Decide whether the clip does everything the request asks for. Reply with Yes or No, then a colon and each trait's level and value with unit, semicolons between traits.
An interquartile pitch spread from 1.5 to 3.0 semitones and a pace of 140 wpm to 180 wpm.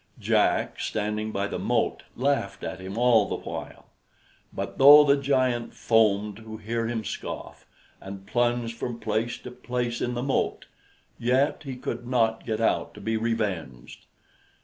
Yes: narrow, 2.5 semitones; average, 155 wpm